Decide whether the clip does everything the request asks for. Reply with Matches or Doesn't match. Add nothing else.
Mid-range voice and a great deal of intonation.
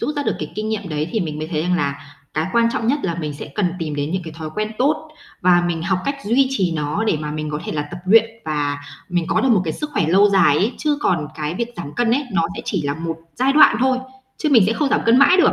Matches